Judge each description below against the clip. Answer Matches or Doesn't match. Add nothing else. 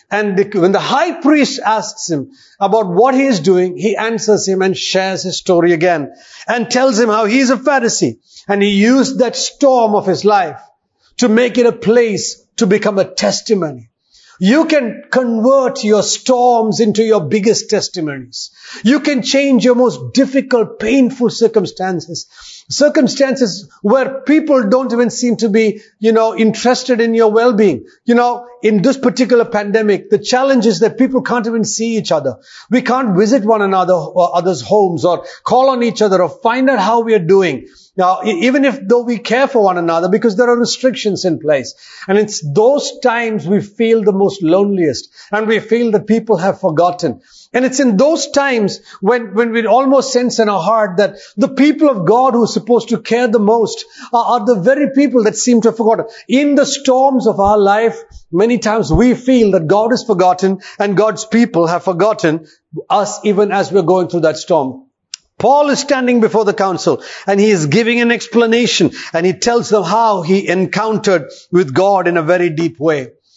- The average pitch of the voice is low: Doesn't match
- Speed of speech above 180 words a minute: Matches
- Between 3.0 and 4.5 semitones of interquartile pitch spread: Matches